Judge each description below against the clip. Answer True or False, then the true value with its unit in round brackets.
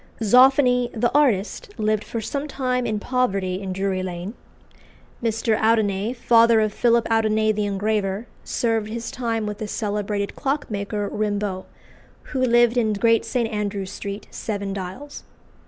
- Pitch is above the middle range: True (215 Hz)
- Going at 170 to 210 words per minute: False (140 wpm)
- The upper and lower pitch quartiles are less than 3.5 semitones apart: True (2.9 semitones)